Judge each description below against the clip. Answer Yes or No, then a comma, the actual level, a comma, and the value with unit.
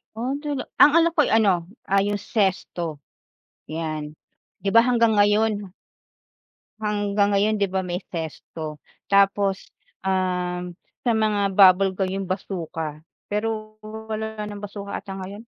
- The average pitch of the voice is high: Yes, high, 200 Hz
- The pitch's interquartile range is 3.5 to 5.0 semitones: No, average, 2.8 semitones